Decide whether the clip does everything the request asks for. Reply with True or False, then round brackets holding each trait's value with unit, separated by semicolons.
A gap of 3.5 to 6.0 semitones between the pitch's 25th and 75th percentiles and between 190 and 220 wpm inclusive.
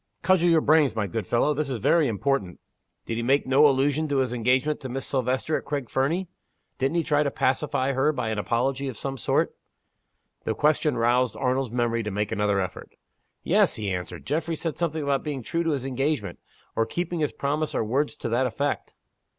True (4.1 semitones; 205 wpm)